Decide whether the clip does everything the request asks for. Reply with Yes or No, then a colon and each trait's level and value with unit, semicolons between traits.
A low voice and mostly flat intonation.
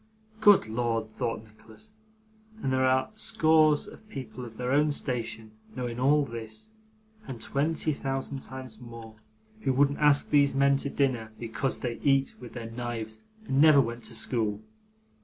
No: low, 130 Hz; average, 3.4 semitones